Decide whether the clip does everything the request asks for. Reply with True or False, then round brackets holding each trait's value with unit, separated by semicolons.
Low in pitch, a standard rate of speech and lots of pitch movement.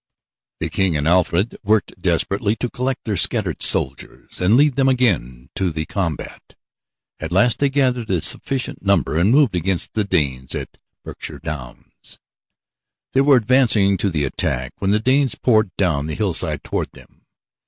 True (100 Hz; 165 wpm; 7.4 semitones)